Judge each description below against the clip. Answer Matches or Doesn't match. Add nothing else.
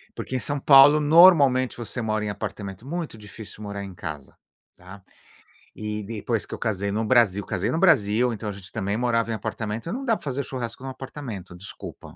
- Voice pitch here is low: Matches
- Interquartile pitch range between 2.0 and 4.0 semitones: Doesn't match